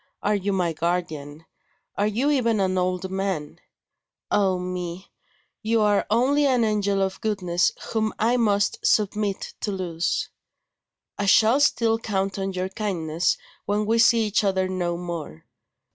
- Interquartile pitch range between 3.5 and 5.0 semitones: No, average, 3.1 semitones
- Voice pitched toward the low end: No, high, 195 Hz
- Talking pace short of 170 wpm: Yes, average, 145 wpm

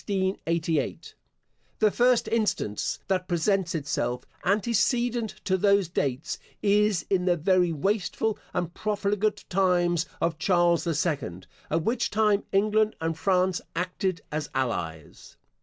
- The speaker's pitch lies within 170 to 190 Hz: Yes, medium, 185 Hz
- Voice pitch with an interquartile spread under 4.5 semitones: Yes, average, 4.1 semitones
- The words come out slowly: Yes, slow, 125 wpm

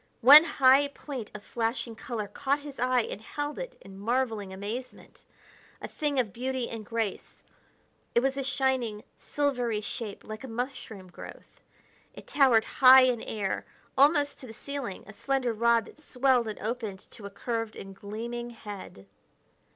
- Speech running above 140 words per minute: Yes, average, 160 wpm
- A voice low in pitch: No, high, 240 Hz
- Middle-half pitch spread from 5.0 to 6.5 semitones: No, average, 3.7 semitones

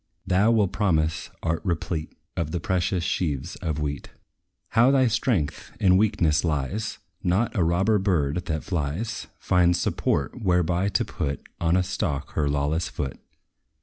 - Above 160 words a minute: No, average, 150 wpm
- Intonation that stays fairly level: No, average, 4.0 semitones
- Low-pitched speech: Yes, very low, 85 Hz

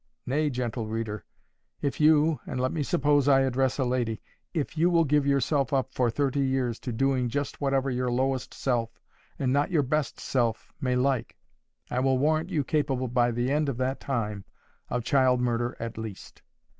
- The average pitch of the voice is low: Yes, low, 130 Hz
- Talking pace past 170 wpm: Yes, average, 180 wpm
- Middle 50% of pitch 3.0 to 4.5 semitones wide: No, narrow, 2.6 semitones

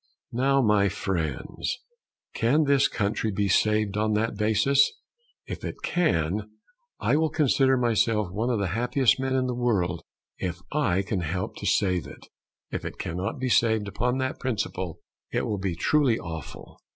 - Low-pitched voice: Yes, low, 110 Hz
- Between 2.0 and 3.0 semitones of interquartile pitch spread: No, average, 5.0 semitones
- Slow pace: No, average, 165 wpm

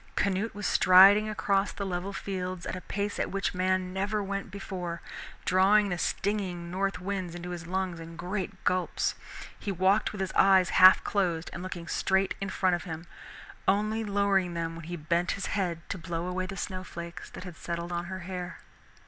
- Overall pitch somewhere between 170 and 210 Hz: Yes, medium, 185 Hz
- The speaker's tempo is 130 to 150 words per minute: No, average, 190 wpm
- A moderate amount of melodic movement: No, narrow, 2.1 semitones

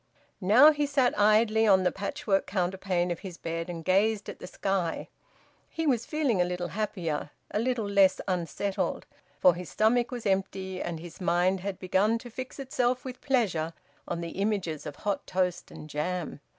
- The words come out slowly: No, average, 175 wpm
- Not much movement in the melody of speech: No, average, 4.1 semitones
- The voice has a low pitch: No, high, 195 Hz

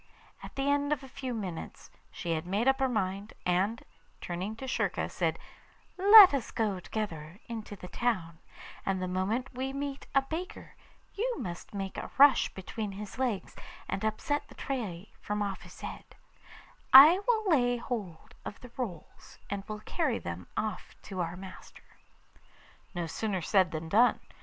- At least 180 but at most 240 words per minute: No, average, 165 wpm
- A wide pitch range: Yes, wide, 6.2 semitones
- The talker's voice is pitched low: No, high, 215 Hz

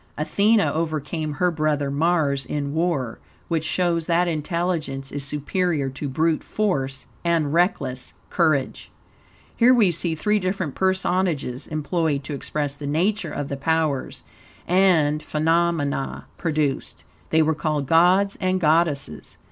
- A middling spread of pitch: Yes, average, 3.5 semitones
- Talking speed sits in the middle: No, slow, 130 wpm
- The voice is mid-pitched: Yes, medium, 160 Hz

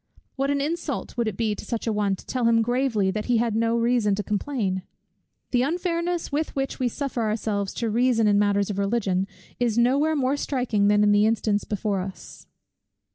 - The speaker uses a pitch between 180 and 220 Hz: No, high, 230 Hz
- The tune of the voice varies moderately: Yes, average, 3.8 semitones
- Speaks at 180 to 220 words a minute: Yes, fast, 205 wpm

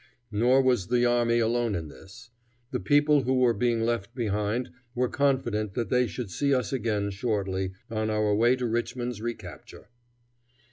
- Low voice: Yes, low, 120 Hz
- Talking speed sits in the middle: Yes, average, 160 wpm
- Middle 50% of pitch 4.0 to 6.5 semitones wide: No, average, 2.8 semitones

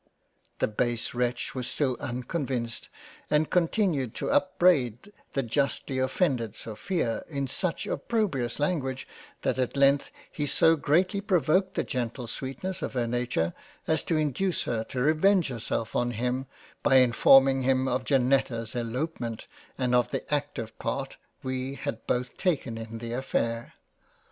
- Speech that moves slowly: No, average, 145 wpm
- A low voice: Yes, low, 130 Hz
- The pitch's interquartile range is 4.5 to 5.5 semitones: No, average, 4.1 semitones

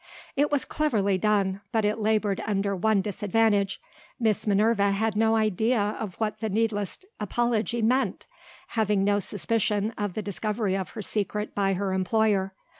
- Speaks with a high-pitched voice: Yes, high, 210 Hz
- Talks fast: No, average, 155 wpm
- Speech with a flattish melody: Yes, narrow, 1.9 semitones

